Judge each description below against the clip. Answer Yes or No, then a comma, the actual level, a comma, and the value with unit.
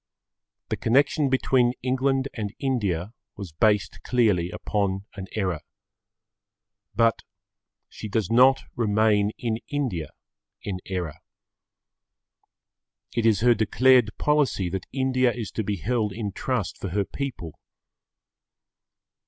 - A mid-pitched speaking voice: No, low, 110 Hz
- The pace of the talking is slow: Yes, slow, 115 wpm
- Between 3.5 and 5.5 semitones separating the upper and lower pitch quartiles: Yes, average, 4.6 semitones